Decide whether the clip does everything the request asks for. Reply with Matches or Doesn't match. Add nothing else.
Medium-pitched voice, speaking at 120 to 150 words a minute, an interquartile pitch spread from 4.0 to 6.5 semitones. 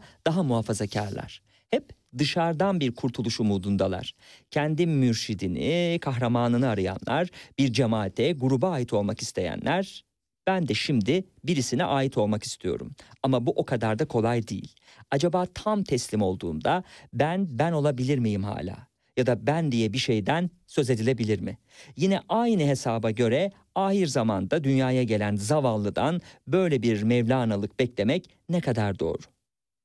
Doesn't match